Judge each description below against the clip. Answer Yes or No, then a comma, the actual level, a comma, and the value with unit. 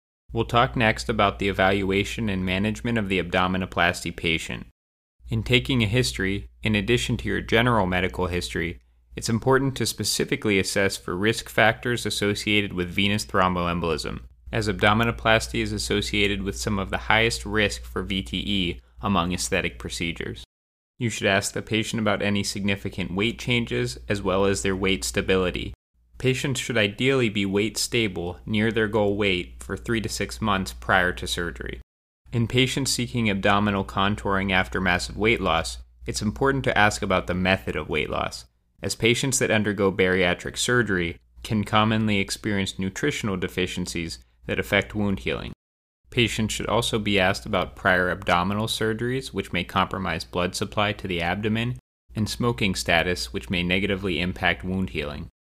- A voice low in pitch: Yes, low, 100 Hz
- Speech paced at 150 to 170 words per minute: Yes, average, 155 wpm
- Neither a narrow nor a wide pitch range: Yes, average, 3.4 semitones